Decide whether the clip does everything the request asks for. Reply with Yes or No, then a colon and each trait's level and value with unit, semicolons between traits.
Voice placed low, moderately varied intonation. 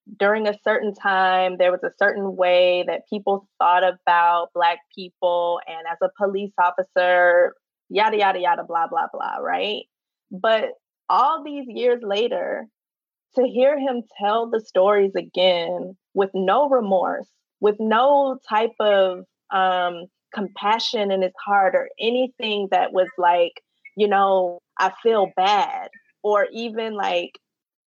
No: high, 200 Hz; average, 4.0 semitones